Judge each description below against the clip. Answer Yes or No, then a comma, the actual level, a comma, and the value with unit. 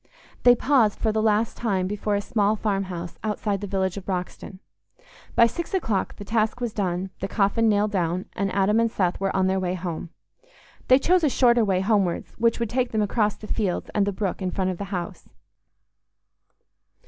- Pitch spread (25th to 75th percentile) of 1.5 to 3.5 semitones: Yes, average, 2.9 semitones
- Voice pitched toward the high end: Yes, high, 205 Hz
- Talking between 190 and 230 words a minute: Yes, average, 195 wpm